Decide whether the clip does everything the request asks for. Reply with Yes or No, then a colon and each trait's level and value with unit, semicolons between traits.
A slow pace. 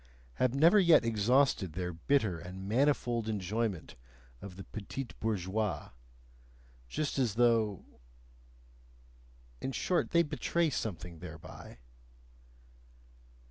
Yes: slow, 100 wpm